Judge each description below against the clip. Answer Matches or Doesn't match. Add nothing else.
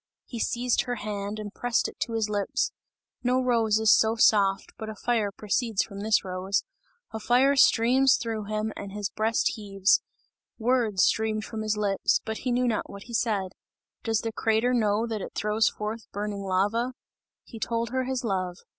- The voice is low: Doesn't match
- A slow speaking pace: Doesn't match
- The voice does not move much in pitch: Matches